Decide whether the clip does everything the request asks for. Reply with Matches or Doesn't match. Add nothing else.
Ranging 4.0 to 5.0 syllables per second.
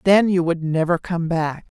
Matches